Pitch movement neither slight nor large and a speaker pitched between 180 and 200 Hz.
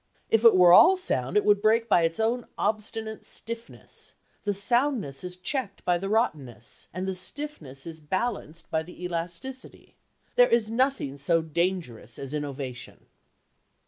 No: wide, 6.2 semitones; medium, 185 Hz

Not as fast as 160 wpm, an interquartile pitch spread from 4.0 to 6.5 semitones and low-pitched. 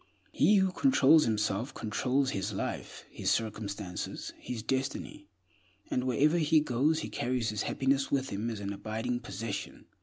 Yes: average, 150 wpm; average, 4.6 semitones; low, 125 Hz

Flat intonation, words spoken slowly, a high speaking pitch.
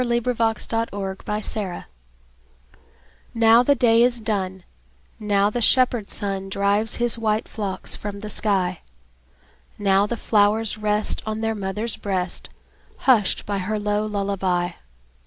Yes: narrow, 2.3 semitones; slow, 130 wpm; high, 210 Hz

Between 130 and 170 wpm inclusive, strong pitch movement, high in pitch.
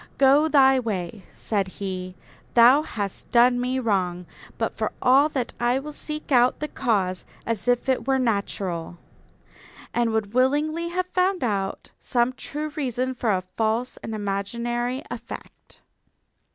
No: average, 145 wpm; average, 4.8 semitones; high, 240 Hz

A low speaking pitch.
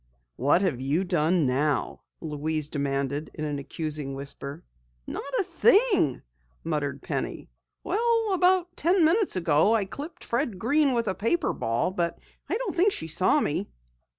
No: medium, 175 Hz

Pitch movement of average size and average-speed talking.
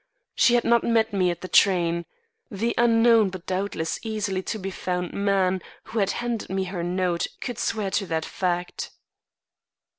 Yes: average, 3.6 semitones; average, 170 wpm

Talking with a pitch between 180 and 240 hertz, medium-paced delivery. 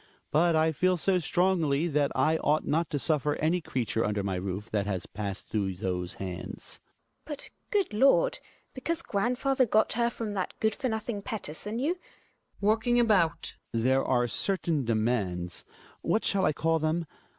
No: medium, 160 Hz; average, 170 wpm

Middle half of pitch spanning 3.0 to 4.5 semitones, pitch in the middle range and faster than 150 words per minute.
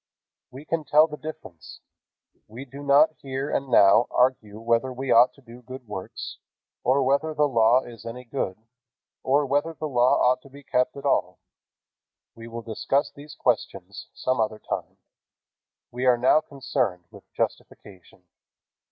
No: average, 3.4 semitones; low, 130 Hz; average, 160 wpm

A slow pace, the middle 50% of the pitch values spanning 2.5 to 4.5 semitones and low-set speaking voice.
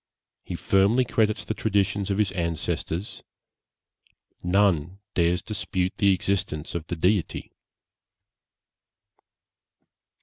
Yes: slow, 95 wpm; average, 2.9 semitones; very low, 95 Hz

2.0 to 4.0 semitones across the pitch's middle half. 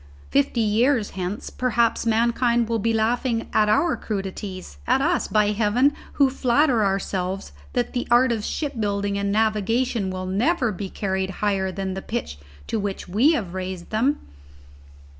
Yes: average, 3.7 semitones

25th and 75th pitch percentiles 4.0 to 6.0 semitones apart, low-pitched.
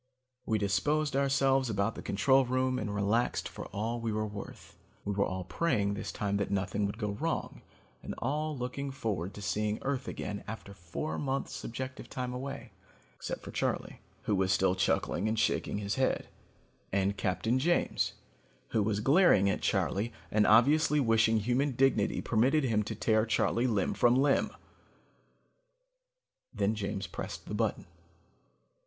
Yes: average, 4.6 semitones; low, 110 Hz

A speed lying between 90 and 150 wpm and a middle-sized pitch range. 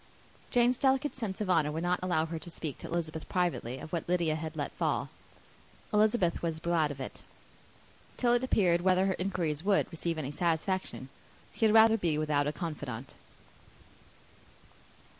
No: average, 165 wpm; average, 3.7 semitones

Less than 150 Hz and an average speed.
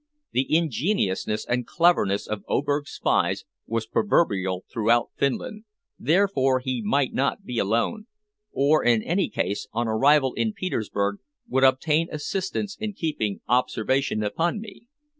No: low, 135 Hz; slow, 130 wpm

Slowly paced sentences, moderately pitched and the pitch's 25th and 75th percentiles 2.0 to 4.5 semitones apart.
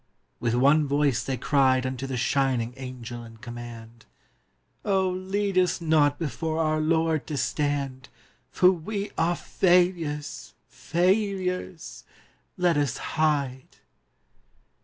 No: slow, 115 wpm; medium, 150 Hz; average, 5.2 semitones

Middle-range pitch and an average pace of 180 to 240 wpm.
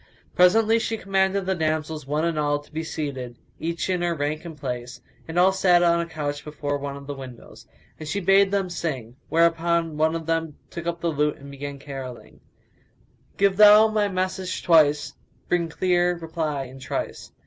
Yes: medium, 165 Hz; average, 190 wpm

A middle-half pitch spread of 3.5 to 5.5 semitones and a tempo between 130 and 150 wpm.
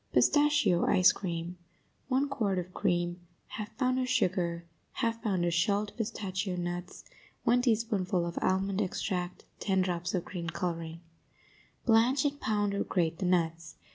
Yes: average, 4.4 semitones; average, 145 wpm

